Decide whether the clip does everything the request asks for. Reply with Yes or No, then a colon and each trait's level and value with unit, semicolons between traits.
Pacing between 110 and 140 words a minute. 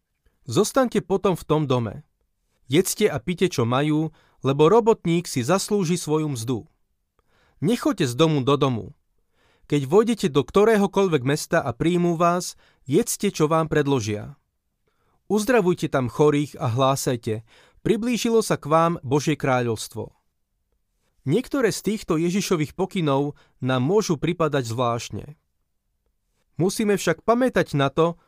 Yes: average, 125 wpm